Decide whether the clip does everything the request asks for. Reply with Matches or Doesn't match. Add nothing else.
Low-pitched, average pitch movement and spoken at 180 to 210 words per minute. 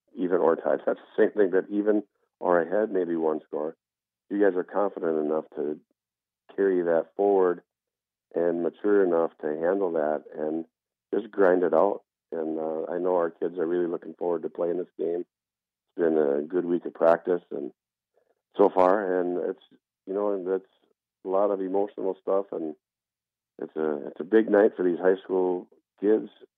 Matches